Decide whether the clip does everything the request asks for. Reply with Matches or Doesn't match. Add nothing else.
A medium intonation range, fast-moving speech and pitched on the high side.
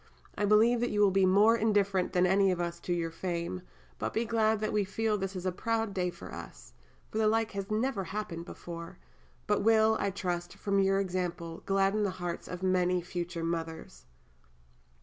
Doesn't match